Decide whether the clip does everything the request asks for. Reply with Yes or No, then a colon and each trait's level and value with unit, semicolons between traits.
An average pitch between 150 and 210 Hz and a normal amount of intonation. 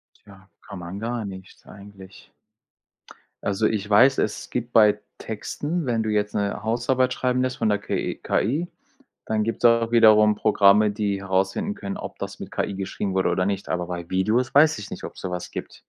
No: low, 105 Hz; average, 3.0 semitones